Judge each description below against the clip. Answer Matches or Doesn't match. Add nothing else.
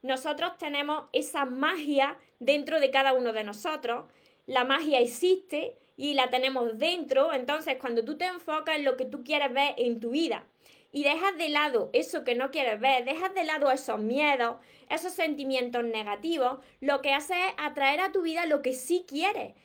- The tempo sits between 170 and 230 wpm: Matches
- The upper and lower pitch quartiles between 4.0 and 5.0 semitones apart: Doesn't match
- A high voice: Matches